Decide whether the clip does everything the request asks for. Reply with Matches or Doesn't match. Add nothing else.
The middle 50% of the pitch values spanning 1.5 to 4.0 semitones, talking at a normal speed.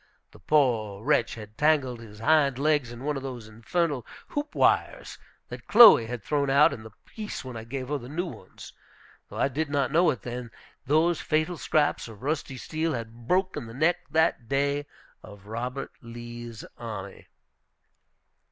Doesn't match